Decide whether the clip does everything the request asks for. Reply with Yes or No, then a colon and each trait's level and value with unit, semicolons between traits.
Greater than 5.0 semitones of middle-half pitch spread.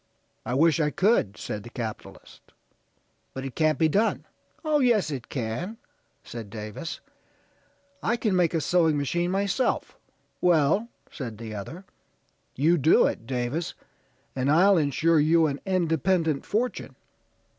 Yes: wide, 5.5 semitones